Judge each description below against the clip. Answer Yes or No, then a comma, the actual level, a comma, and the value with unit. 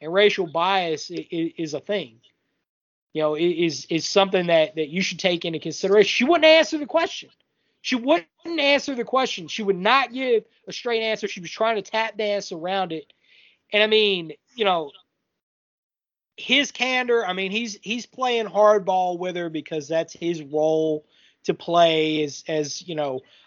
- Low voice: No, high, 190 Hz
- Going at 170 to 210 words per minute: Yes, average, 175 wpm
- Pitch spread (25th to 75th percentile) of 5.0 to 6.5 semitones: Yes, wide, 5.6 semitones